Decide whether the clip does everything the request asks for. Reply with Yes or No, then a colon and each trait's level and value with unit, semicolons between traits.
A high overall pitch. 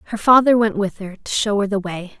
Yes: high, 210 Hz